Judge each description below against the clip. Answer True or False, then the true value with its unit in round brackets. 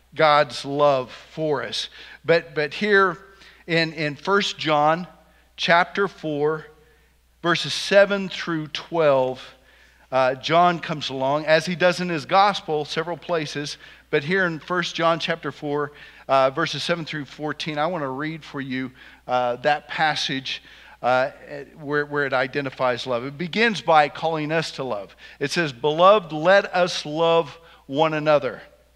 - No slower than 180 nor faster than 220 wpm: False (145 wpm)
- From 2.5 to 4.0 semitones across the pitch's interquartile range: True (2.8 semitones)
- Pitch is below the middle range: False (155 Hz)